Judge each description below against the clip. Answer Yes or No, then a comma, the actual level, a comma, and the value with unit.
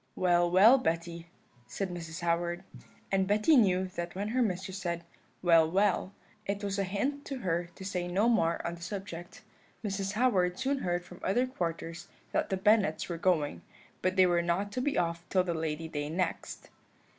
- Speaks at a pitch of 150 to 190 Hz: Yes, medium, 185 Hz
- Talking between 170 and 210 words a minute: Yes, average, 185 wpm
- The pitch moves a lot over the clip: No, average, 2.8 semitones